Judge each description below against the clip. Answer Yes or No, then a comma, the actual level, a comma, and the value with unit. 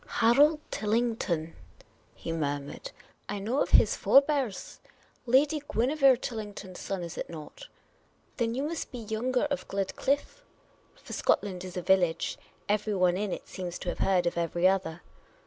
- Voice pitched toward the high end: Yes, high, 205 Hz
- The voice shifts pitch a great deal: Yes, wide, 6.1 semitones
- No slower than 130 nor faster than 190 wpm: Yes, average, 165 wpm